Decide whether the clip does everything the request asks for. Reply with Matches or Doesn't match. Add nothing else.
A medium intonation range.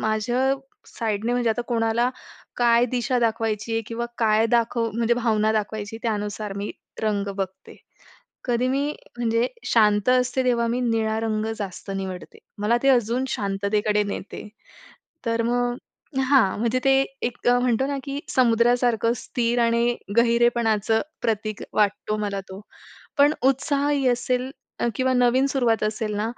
Doesn't match